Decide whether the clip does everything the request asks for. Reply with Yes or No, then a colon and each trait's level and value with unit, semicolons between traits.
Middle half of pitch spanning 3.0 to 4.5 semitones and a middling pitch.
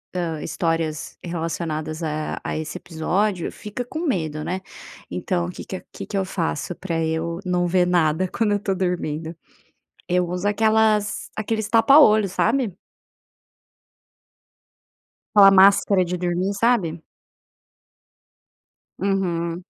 Yes: average, 3.4 semitones; medium, 180 Hz